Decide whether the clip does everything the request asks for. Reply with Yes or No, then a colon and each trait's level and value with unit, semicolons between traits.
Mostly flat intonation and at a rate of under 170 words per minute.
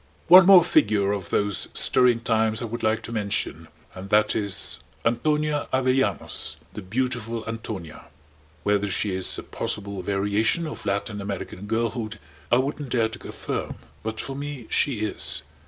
No: average, 3.8 semitones; average, 155 wpm